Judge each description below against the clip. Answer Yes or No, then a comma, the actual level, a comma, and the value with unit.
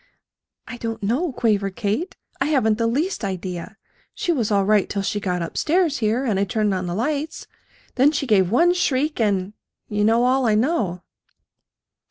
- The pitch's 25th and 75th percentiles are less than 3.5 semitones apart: No, average, 5.3 semitones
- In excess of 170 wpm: Yes, average, 185 wpm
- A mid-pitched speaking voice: No, high, 225 Hz